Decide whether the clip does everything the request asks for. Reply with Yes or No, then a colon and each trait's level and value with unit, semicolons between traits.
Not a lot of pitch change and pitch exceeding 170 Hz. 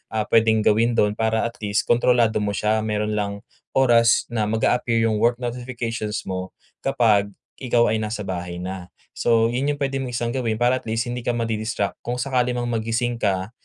No: narrow, 2.2 semitones; low, 115 Hz